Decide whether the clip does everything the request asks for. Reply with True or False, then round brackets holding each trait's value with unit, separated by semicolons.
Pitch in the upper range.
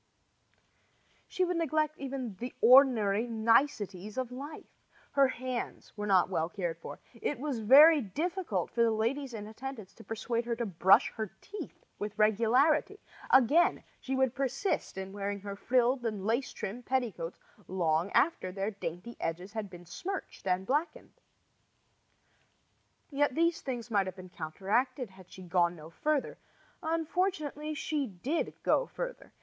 True (235 Hz)